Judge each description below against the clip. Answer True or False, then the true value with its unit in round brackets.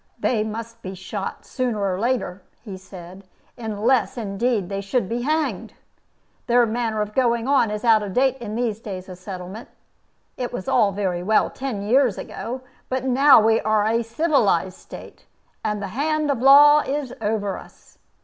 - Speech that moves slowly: False (170 wpm)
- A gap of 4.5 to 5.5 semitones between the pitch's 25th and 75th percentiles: False (4.1 semitones)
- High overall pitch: True (225 Hz)